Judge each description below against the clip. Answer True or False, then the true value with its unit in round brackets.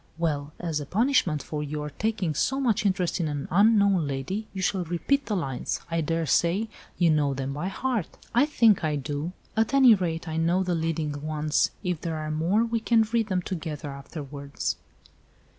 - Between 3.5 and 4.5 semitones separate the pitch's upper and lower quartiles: False (5.6 semitones)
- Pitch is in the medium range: True (170 Hz)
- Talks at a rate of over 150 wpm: True (185 wpm)